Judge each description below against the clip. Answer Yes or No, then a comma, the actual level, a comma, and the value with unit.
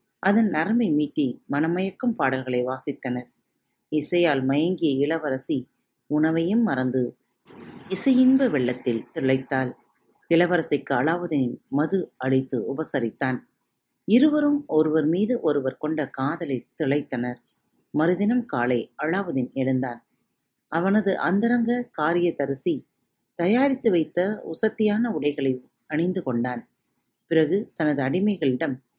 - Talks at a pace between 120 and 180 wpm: No, average, 90 wpm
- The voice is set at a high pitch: No, medium, 155 Hz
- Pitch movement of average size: No, wide, 6.7 semitones